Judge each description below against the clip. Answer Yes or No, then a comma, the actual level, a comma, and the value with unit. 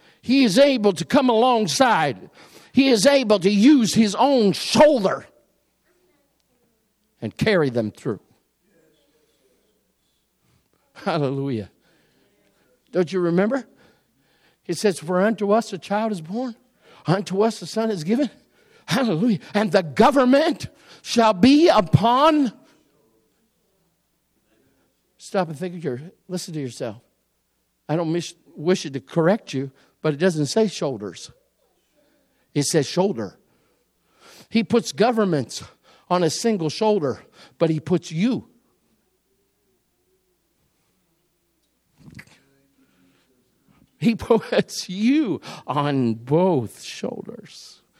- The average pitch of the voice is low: No, high, 190 Hz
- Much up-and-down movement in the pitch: Yes, wide, 6.3 semitones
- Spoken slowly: Yes, slow, 105 wpm